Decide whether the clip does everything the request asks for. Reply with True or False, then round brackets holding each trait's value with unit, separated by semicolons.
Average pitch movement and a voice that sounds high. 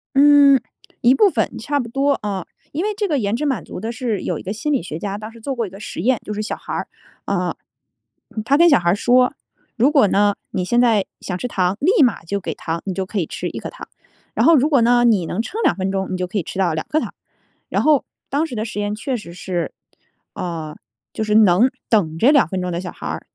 False (6.3 semitones; 220 Hz)